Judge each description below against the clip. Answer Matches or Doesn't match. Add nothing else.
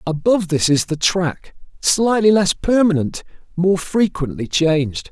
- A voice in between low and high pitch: Matches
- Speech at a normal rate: Doesn't match